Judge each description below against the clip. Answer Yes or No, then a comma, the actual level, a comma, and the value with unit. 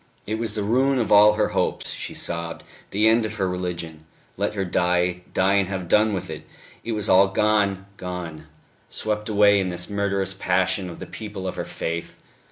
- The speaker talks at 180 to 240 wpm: Yes, average, 195 wpm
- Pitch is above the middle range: No, very low, 95 Hz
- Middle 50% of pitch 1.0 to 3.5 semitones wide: Yes, average, 2.8 semitones